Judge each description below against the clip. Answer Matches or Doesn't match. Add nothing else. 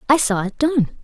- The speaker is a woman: Matches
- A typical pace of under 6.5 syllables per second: Matches